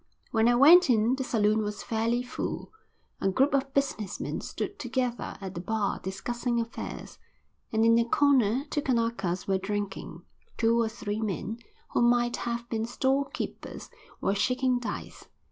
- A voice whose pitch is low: No, high, 230 Hz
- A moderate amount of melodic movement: Yes, average, 3.1 semitones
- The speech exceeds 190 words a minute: No, average, 160 wpm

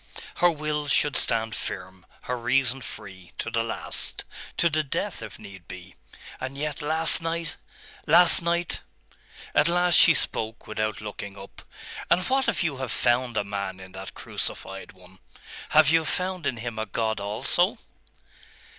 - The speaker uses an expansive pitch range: Yes, wide, 7.7 semitones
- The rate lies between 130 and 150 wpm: No, average, 160 wpm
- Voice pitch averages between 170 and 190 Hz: No, low, 125 Hz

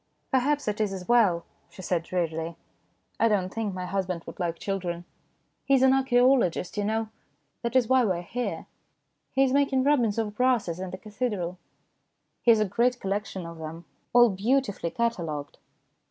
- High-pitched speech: Yes, high, 210 Hz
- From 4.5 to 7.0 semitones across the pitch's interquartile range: Yes, wide, 5.4 semitones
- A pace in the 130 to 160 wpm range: No, average, 185 wpm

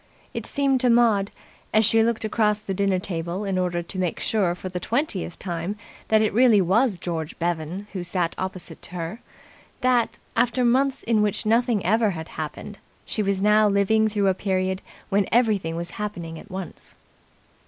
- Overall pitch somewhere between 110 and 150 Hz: No, high, 200 Hz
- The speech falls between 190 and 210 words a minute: No, average, 175 wpm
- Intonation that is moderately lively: Yes, average, 3.5 semitones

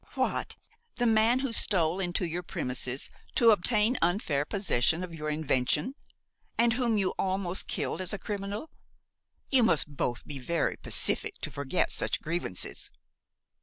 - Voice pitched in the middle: Yes, medium, 180 Hz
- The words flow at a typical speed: Yes, average, 145 wpm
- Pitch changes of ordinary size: No, wide, 6.1 semitones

